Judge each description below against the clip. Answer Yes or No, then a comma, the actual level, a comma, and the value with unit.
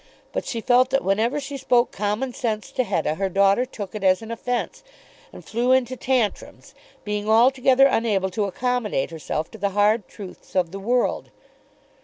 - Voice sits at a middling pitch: No, high, 220 Hz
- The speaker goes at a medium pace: Yes, average, 175 wpm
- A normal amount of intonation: Yes, average, 4.0 semitones